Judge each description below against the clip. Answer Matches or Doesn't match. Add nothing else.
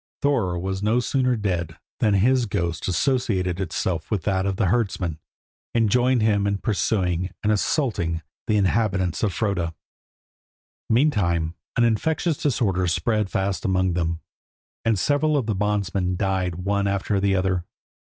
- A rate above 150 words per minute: Doesn't match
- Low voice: Matches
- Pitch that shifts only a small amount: Doesn't match